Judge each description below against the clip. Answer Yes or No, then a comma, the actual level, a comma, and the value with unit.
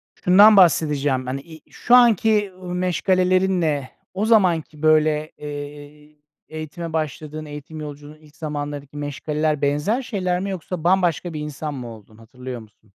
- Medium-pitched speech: Yes, medium, 155 Hz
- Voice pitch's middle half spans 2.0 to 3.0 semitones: No, average, 3.9 semitones